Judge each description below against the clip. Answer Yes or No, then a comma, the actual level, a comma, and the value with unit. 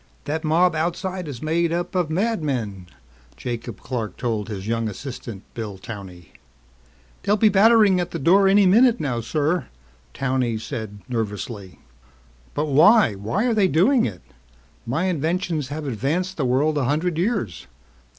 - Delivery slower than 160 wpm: Yes, average, 150 wpm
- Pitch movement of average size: No, wide, 7.9 semitones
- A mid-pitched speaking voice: Yes, medium, 150 Hz